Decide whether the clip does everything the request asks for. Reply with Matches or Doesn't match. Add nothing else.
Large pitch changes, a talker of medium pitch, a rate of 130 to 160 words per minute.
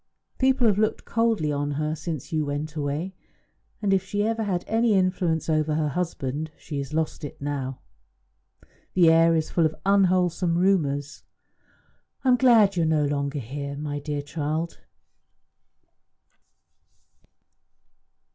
Doesn't match